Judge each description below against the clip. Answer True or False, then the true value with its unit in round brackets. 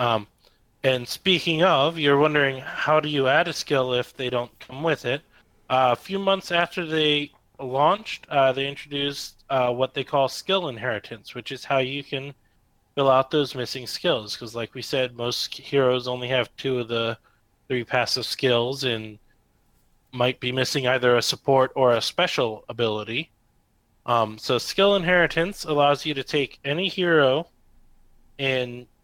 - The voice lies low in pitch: True (130 Hz)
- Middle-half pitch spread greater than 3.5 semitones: False (3.1 semitones)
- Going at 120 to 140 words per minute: False (165 wpm)